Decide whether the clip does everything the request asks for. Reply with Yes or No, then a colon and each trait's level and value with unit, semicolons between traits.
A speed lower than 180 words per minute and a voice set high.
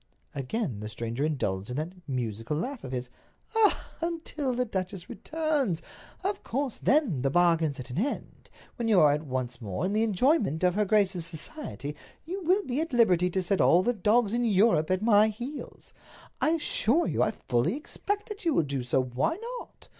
No: average, 185 wpm; high, 195 Hz